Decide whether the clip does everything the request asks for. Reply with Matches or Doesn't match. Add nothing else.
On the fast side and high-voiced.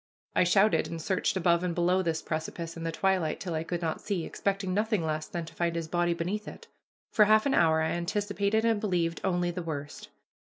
Doesn't match